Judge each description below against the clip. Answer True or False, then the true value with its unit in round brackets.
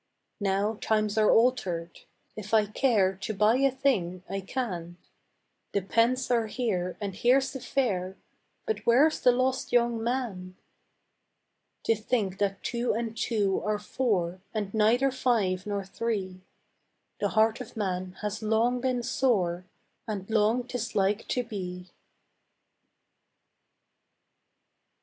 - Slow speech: True (130 wpm)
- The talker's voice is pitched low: False (215 Hz)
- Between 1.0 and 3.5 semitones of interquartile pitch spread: False (4.0 semitones)